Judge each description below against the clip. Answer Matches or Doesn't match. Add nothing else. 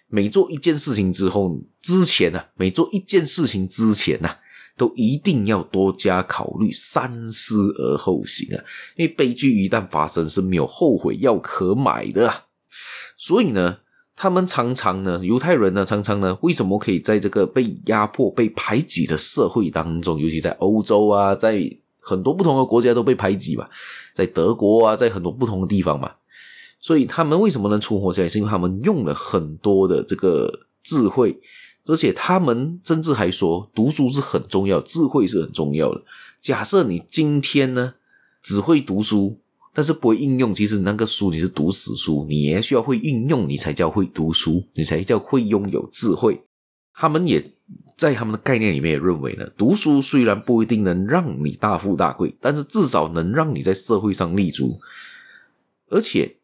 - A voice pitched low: Matches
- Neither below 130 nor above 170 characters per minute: Doesn't match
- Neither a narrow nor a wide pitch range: Doesn't match